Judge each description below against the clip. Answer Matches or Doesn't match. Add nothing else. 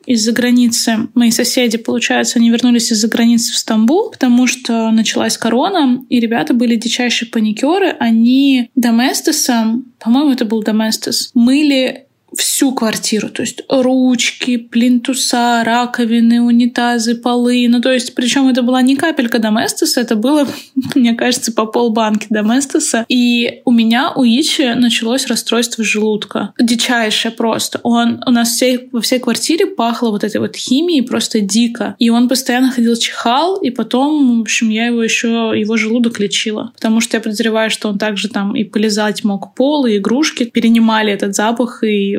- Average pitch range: Doesn't match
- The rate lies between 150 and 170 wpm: Matches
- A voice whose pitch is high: Matches